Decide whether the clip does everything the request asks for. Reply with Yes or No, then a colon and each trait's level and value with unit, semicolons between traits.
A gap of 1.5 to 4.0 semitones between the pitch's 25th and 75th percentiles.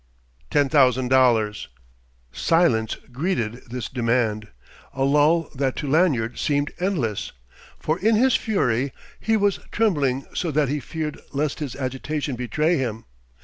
No: average, 4.5 semitones